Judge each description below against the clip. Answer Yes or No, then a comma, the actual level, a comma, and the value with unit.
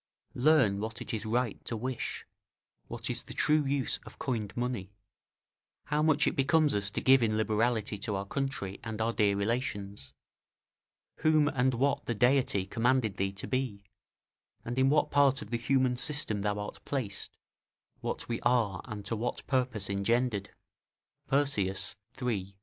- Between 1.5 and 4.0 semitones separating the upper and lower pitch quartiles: No, average, 4.4 semitones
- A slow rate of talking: No, average, 160 wpm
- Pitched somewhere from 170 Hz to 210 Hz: No, low, 120 Hz